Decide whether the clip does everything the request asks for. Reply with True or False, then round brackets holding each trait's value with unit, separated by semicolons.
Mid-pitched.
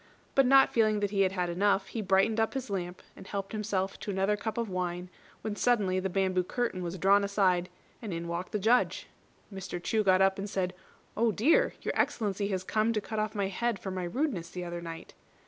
False (195 Hz)